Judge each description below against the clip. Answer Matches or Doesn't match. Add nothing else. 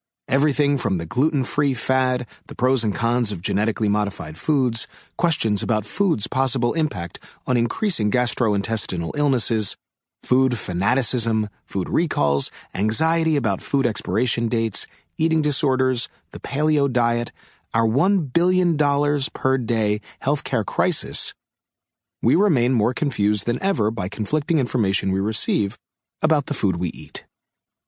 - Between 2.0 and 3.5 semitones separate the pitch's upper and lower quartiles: Doesn't match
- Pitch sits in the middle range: Doesn't match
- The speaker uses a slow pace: Matches